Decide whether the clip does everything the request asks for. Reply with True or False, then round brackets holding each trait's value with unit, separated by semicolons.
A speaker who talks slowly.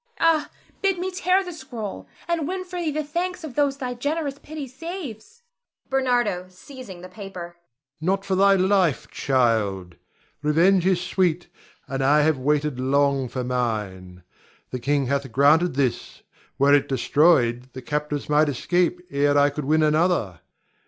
False (155 wpm)